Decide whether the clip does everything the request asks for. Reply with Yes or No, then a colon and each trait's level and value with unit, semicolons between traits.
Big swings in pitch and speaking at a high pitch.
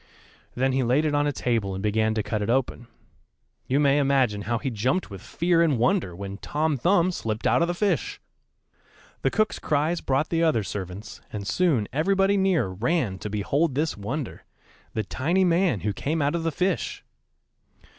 No: wide, 7.6 semitones; low, 135 Hz